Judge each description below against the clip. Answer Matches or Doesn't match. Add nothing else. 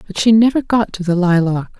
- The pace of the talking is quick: Matches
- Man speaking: Doesn't match